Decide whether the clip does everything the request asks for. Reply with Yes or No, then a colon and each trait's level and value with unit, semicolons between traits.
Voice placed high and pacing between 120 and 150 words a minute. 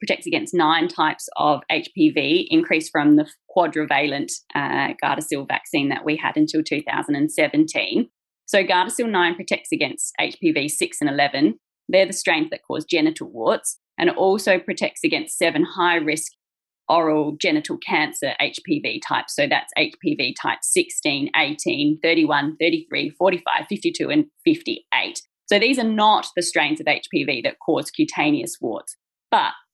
Yes: high, 225 Hz; average, 145 wpm